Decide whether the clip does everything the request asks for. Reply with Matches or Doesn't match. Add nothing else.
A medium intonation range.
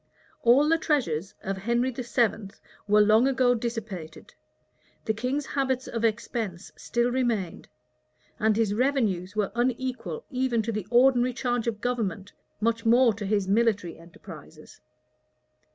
Matches